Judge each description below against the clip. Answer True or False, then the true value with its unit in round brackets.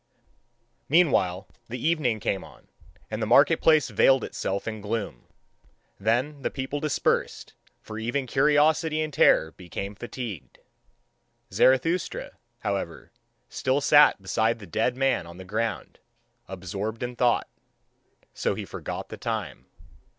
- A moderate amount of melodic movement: False (5.8 semitones)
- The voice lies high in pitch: False (120 Hz)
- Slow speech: True (130 wpm)